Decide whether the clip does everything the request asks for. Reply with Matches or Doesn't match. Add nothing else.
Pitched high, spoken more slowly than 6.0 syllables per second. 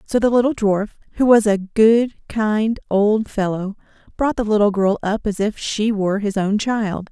Matches